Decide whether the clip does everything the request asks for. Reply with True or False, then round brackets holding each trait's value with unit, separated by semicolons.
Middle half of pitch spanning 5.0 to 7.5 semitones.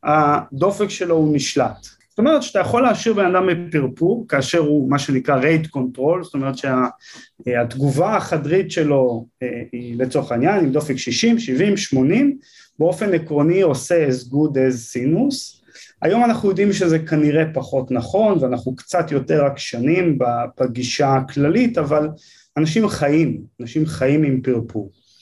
True (5.6 semitones)